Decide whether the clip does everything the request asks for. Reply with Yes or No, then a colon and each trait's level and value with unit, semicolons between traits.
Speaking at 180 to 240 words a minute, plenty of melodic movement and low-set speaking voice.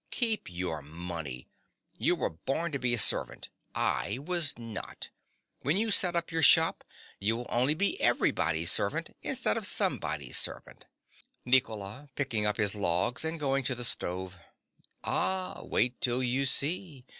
No: average, 155 wpm; wide, 7.5 semitones; low, 125 Hz